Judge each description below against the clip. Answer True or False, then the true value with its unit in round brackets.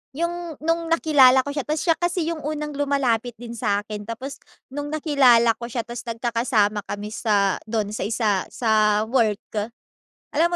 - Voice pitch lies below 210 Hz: False (240 Hz)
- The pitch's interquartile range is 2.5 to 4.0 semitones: False (5.4 semitones)